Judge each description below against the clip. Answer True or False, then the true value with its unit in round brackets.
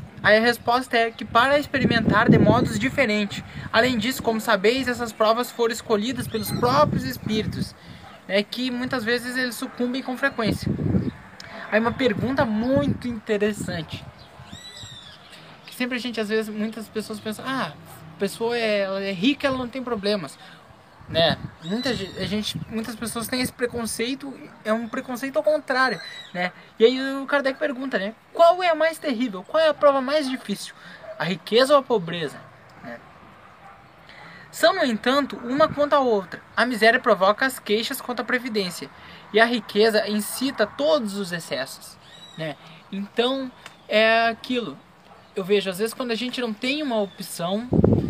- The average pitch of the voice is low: False (230 Hz)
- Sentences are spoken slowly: False (160 wpm)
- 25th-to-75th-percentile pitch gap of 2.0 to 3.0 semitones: False (3.7 semitones)